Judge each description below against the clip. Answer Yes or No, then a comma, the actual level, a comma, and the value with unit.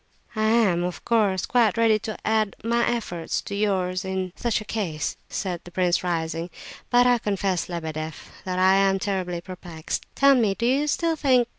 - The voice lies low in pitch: No, high, 195 Hz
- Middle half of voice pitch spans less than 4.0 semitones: No, average, 4.4 semitones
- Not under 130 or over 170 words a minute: No, average, 180 wpm